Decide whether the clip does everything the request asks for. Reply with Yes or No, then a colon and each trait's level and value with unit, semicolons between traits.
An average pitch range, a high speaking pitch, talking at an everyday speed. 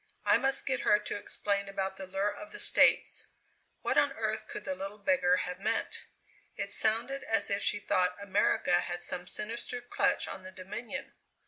Yes: average, 4.0 semitones; high, 205 Hz; average, 185 wpm